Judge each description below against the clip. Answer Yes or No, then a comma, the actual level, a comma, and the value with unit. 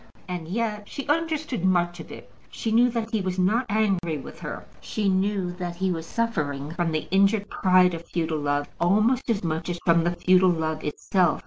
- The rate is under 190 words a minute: No, average, 200 wpm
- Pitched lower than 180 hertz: No, medium, 185 Hz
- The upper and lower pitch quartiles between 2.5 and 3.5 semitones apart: No, average, 4.3 semitones